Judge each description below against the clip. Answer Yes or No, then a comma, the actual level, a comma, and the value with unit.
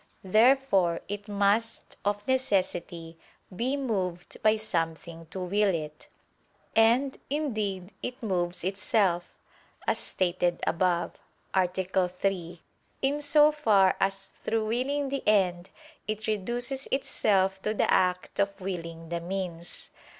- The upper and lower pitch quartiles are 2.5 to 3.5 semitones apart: No, average, 4.0 semitones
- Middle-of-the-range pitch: No, high, 195 Hz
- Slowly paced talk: Yes, slow, 120 wpm